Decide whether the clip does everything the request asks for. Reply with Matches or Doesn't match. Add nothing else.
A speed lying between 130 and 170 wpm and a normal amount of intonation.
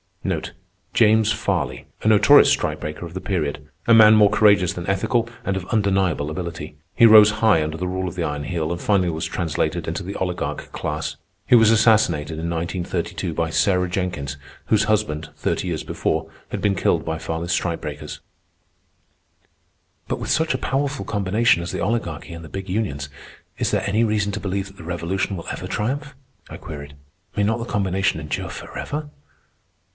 Doesn't match